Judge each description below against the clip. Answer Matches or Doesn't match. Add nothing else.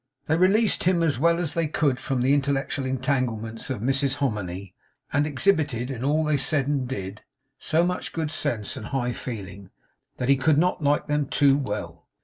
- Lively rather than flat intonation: Doesn't match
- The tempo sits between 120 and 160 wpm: Doesn't match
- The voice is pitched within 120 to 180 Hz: Matches